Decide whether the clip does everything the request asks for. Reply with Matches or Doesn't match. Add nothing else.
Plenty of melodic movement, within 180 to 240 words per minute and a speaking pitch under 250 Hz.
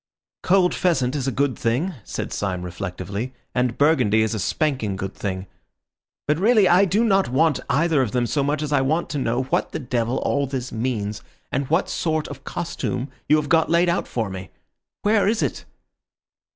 Matches